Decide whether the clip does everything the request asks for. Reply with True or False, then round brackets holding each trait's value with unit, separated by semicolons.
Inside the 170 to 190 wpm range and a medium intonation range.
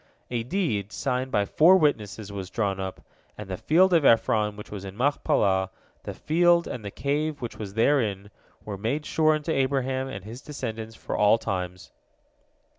False (175 wpm; 6.2 semitones)